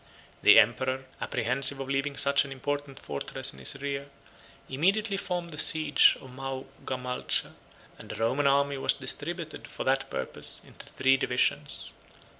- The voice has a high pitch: No, low, 135 Hz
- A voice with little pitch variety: Yes, narrow, 1.6 semitones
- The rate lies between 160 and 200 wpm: No, average, 145 wpm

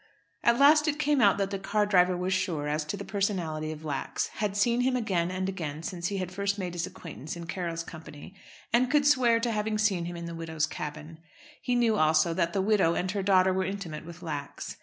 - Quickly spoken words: Yes, fast, 230 wpm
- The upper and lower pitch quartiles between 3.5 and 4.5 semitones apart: Yes, average, 4.2 semitones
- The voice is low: No, medium, 185 Hz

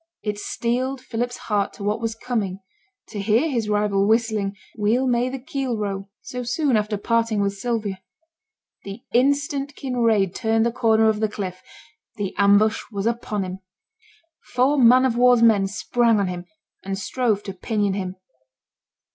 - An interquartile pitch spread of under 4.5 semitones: Yes, average, 3.3 semitones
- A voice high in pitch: Yes, high, 220 Hz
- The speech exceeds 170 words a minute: No, average, 160 wpm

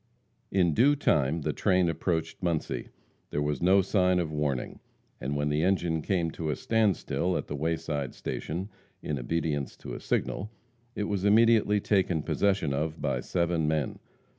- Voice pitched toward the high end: No, very low, 85 Hz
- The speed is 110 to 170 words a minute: Yes, average, 165 wpm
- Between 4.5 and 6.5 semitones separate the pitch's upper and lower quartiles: No, average, 4.1 semitones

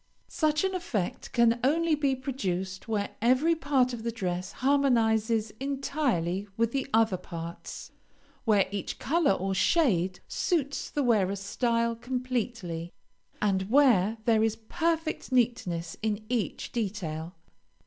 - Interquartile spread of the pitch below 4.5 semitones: No, wide, 5.6 semitones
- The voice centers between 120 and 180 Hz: No, high, 230 Hz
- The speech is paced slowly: Yes, slow, 130 wpm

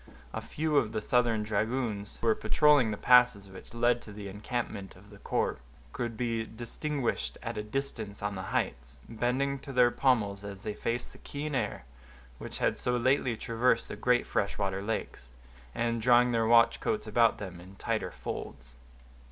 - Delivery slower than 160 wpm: No, average, 180 wpm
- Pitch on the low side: Yes, low, 115 Hz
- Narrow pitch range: No, average, 3.3 semitones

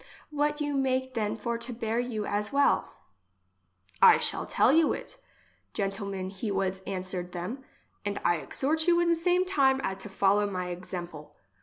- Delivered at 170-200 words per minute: Yes, average, 175 wpm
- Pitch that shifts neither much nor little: No, wide, 6.4 semitones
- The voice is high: Yes, high, 210 Hz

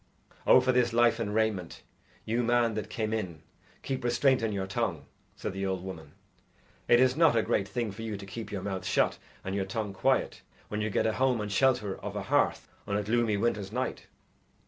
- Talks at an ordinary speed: No, fast, 215 wpm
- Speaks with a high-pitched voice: No, low, 110 Hz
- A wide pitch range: No, average, 3.4 semitones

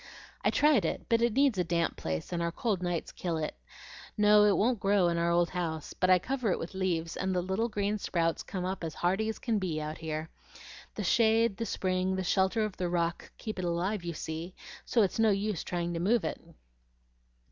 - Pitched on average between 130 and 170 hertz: No, medium, 185 Hz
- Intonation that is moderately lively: Yes, average, 3.8 semitones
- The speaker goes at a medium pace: No, fast, 225 wpm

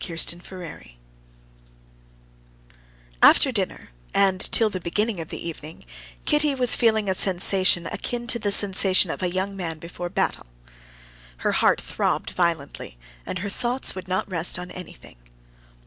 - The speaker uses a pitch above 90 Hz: Yes, medium, 185 Hz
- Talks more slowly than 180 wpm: Yes, average, 145 wpm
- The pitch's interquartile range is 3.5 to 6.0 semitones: No, average, 3.1 semitones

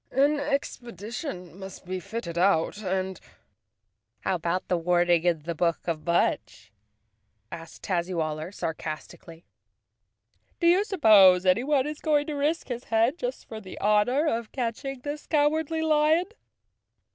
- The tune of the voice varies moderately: No, wide, 8.7 semitones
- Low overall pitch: No, high, 210 Hz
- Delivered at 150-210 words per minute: No, slow, 135 wpm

